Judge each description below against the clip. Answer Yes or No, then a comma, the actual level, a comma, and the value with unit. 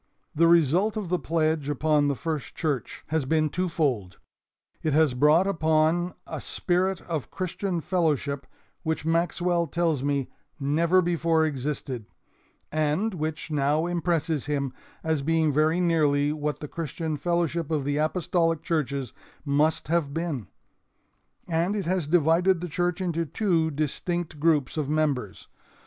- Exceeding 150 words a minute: No, average, 140 wpm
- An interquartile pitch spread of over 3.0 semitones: No, narrow, 2.6 semitones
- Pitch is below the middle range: No, medium, 160 Hz